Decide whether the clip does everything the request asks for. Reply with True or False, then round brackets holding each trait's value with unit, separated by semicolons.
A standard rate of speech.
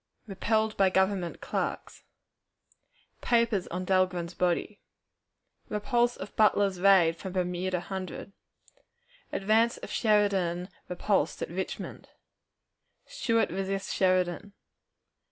False (95 wpm)